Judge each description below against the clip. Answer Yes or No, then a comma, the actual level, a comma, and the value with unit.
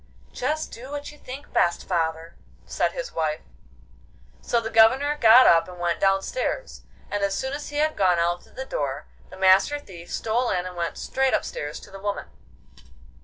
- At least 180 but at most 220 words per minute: Yes, average, 185 wpm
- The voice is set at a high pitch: Yes, high, 200 Hz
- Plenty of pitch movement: Yes, wide, 7.3 semitones